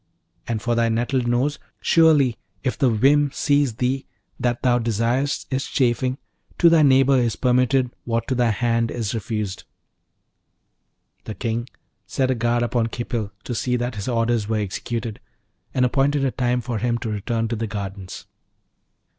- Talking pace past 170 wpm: No, average, 165 wpm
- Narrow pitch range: Yes, narrow, 2.3 semitones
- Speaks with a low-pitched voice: Yes, low, 120 Hz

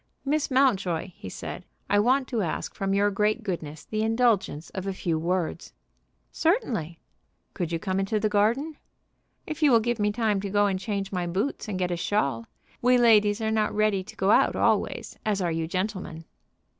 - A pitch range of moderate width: Yes, average, 3.5 semitones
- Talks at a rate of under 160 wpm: No, average, 195 wpm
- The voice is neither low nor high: No, high, 205 Hz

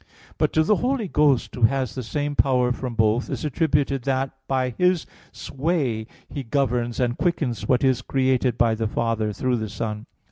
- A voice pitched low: Yes, low, 130 Hz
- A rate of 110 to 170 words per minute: No, average, 180 wpm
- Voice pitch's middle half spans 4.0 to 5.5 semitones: No, average, 3.4 semitones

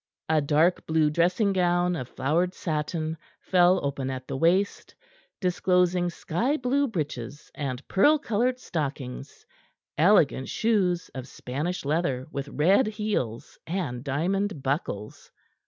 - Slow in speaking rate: Yes, slow, 120 wpm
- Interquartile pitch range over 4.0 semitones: Yes, average, 5.2 semitones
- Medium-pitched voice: Yes, medium, 170 Hz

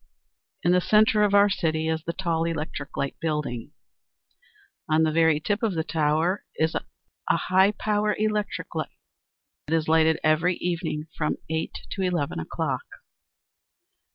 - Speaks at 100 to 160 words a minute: Yes, average, 150 wpm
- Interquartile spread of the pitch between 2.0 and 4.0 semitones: Yes, average, 3.6 semitones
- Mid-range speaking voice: Yes, medium, 165 Hz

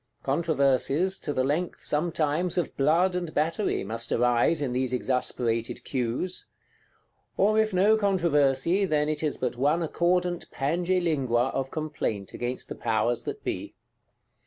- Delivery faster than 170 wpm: No, average, 140 wpm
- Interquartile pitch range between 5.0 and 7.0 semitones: Yes, wide, 5.4 semitones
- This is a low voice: No, medium, 150 Hz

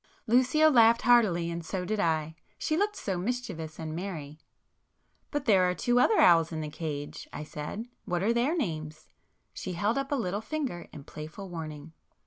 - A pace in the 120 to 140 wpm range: No, average, 165 wpm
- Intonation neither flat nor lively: No, wide, 7.2 semitones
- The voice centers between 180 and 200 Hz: Yes, medium, 185 Hz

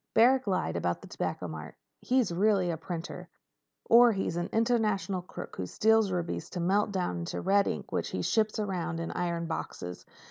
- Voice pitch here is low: No, medium, 185 Hz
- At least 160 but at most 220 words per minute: Yes, average, 180 wpm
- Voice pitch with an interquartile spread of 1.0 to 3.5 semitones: No, average, 4.4 semitones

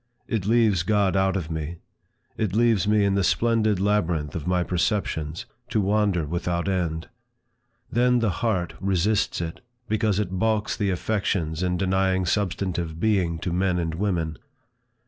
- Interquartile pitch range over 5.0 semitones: No, average, 3.4 semitones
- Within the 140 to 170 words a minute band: Yes, average, 150 wpm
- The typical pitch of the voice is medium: No, very low, 95 Hz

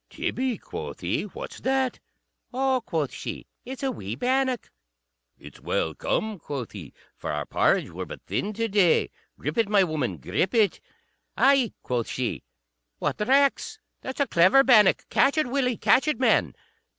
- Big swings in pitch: Yes, wide, 9.0 semitones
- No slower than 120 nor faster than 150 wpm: No, average, 165 wpm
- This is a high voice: Yes, high, 230 Hz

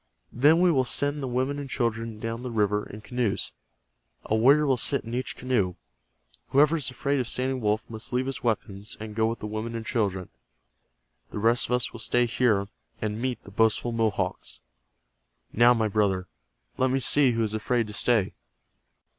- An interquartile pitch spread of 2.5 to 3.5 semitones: Yes, average, 3.0 semitones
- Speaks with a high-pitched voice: No, low, 115 Hz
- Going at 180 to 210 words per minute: Yes, average, 190 wpm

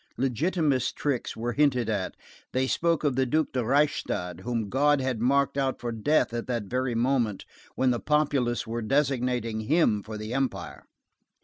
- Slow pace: No, average, 170 wpm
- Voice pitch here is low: Yes, low, 125 Hz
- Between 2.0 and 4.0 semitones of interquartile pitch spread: Yes, average, 3.4 semitones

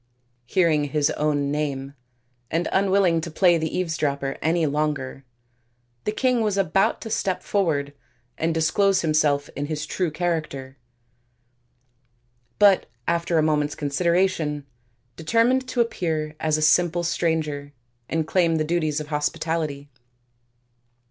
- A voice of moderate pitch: Yes, medium, 160 Hz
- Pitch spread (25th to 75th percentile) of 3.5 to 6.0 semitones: No, average, 3.1 semitones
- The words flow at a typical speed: No, slow, 130 wpm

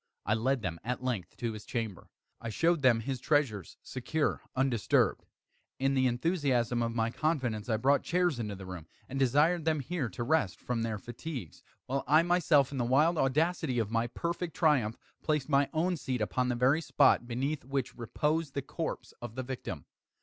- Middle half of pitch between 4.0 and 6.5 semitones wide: Yes, average, 4.6 semitones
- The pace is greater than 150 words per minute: Yes, average, 185 wpm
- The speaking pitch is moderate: No, low, 130 Hz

